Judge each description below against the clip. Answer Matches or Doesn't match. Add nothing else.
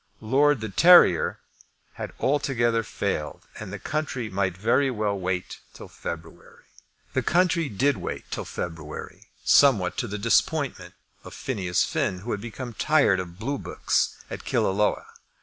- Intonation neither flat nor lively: Doesn't match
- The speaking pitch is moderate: Doesn't match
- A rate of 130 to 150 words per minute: Matches